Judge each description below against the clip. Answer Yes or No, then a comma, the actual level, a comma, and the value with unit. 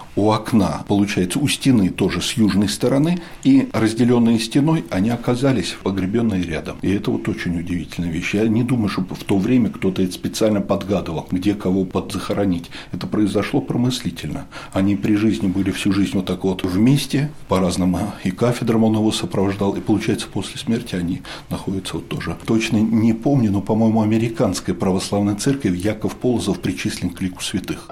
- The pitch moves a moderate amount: Yes, average, 3.6 semitones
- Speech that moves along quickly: Yes, fast, 165 wpm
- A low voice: Yes, low, 100 Hz